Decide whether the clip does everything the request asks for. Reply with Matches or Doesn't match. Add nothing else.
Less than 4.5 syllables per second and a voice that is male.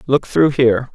Doesn't match